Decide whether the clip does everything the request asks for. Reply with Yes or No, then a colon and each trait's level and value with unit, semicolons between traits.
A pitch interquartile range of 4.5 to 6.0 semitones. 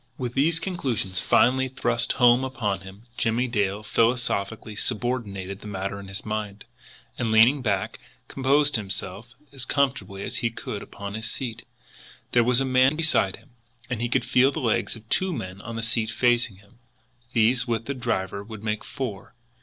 No: average, 4.0 semitones